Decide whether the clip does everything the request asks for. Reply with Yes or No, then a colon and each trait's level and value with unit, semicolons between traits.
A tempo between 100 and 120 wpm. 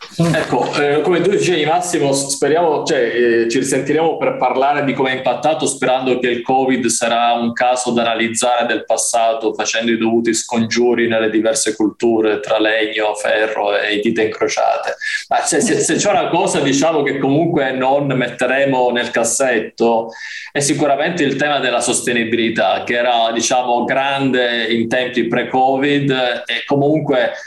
No: average, 155 wpm